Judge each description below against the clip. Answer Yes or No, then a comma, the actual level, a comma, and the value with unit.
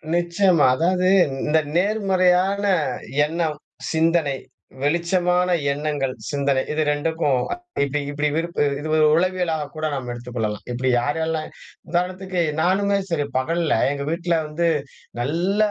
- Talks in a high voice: No, medium, 165 Hz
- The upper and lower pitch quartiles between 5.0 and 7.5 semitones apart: No, average, 3.7 semitones